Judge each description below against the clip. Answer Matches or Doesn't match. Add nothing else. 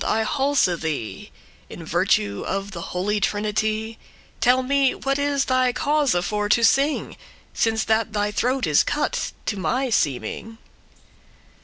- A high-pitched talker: Matches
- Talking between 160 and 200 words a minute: Doesn't match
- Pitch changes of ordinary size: Matches